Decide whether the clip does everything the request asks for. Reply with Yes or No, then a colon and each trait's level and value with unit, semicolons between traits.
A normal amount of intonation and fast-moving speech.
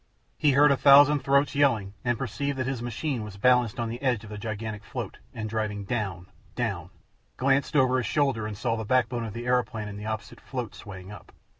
Yes: average, 3.8 semitones; fast, 210 wpm